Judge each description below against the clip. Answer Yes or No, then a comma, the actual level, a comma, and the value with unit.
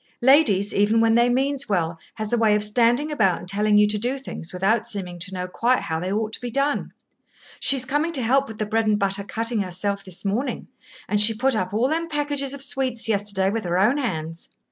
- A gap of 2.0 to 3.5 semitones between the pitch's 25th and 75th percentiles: No, average, 4.7 semitones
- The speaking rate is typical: No, fast, 230 wpm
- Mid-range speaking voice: No, high, 220 Hz